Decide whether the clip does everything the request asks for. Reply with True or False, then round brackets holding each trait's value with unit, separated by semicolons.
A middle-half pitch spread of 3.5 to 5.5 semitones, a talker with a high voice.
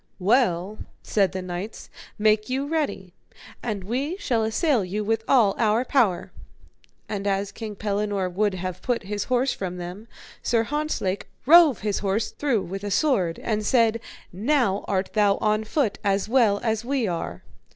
True (3.8 semitones; 215 Hz)